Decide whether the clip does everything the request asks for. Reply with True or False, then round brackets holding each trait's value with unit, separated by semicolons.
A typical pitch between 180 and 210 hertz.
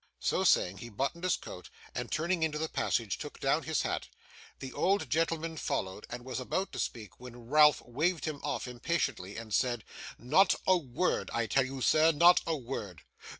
False (135 Hz)